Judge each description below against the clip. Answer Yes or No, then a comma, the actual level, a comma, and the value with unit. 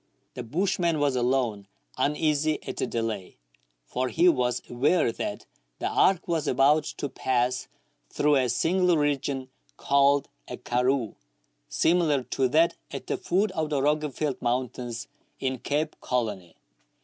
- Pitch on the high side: No, low, 135 Hz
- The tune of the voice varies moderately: Yes, average, 3.7 semitones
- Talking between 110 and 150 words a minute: Yes, slow, 135 wpm